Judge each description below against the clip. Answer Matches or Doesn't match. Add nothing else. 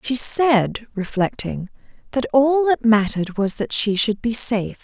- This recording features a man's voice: Doesn't match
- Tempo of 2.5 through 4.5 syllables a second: Matches